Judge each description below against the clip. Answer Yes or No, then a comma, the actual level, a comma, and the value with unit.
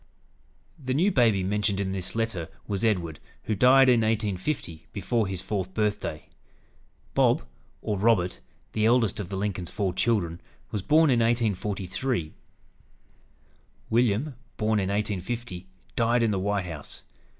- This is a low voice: Yes, low, 105 Hz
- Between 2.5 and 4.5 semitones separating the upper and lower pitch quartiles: Yes, average, 3.6 semitones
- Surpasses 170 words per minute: No, average, 140 wpm